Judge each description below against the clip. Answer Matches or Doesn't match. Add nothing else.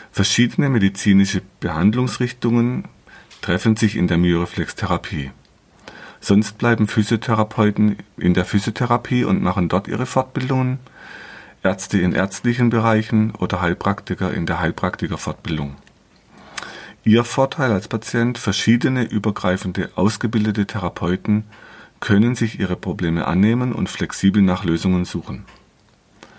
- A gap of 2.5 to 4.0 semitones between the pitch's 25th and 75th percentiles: Doesn't match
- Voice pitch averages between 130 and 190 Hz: Doesn't match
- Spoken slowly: Matches